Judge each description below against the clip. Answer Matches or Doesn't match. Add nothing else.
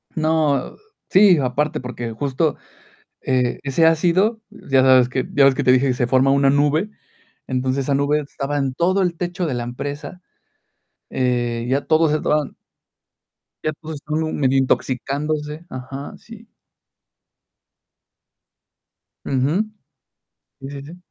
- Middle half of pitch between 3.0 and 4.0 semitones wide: Matches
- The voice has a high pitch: Doesn't match